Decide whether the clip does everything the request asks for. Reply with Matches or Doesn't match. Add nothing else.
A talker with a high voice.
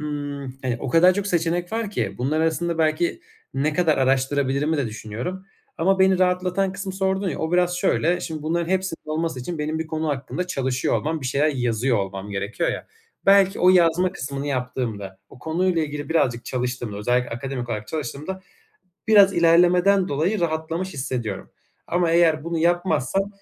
Doesn't match